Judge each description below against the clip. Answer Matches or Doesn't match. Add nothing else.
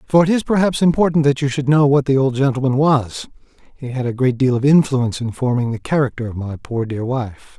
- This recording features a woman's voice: Doesn't match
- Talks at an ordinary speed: Doesn't match